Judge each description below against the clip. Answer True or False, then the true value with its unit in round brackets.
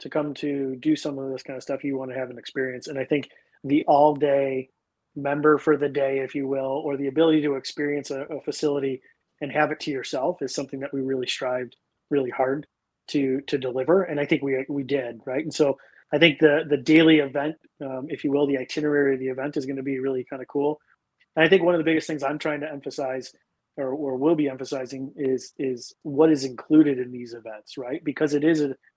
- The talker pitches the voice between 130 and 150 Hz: True (140 Hz)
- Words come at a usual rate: False (235 wpm)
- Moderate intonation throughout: False (2.2 semitones)